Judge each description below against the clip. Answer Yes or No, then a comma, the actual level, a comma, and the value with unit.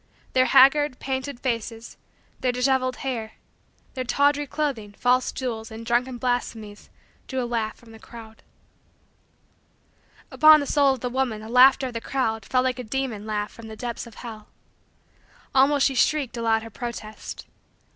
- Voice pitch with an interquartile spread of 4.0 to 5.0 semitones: No, average, 2.9 semitones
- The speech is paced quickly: No, average, 160 wpm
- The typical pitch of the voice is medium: No, high, 245 Hz